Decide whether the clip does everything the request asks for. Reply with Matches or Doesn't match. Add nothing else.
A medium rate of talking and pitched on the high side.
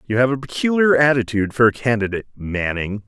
Doesn't match